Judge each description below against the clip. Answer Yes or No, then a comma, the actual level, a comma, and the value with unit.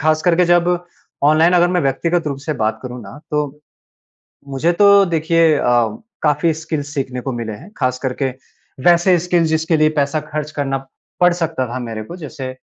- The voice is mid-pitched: Yes, medium, 155 Hz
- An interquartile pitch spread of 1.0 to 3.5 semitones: No, average, 3.9 semitones